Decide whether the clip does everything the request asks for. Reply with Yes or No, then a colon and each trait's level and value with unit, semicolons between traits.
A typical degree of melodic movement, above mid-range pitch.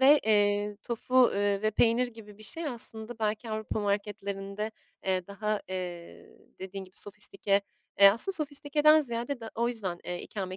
Yes: average, 3.1 semitones; high, 215 Hz